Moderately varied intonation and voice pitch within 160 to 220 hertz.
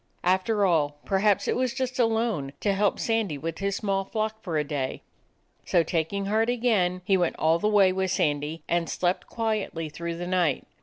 Yes: average, 4.4 semitones; high, 190 Hz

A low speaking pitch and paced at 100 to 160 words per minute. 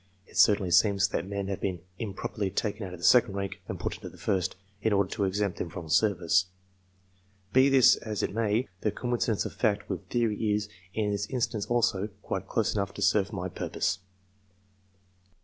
No: low, 100 Hz; average, 185 wpm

